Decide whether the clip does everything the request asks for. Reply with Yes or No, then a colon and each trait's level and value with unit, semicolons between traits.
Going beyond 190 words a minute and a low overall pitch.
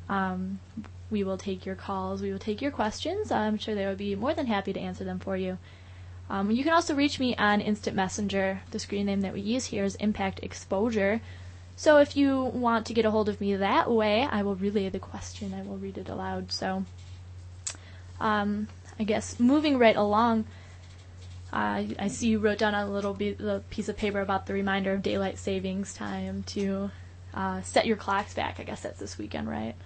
No: fast, 205 wpm; high, 195 Hz